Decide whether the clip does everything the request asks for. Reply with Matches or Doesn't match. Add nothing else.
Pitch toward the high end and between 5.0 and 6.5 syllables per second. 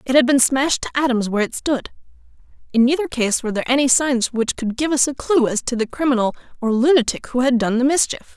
Matches